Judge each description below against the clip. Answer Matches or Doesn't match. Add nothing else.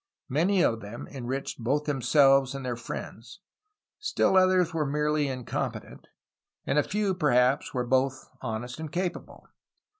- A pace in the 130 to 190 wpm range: Matches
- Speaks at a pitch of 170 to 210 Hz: Doesn't match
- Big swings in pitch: Doesn't match